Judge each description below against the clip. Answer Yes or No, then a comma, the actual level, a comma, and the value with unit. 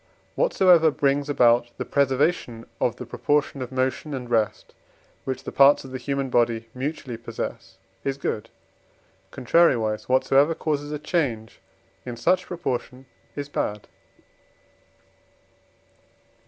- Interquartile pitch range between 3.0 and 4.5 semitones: Yes, average, 3.4 semitones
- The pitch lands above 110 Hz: Yes, low, 135 Hz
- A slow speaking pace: Yes, slow, 120 wpm